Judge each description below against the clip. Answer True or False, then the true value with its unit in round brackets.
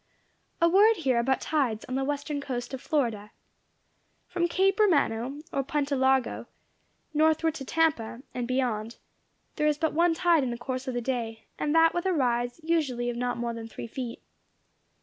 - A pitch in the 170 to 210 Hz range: False (265 Hz)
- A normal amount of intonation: True (4.8 semitones)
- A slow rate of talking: False (180 wpm)